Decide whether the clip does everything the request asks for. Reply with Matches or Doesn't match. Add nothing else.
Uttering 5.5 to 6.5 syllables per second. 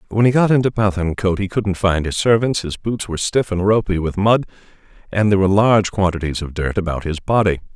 Matches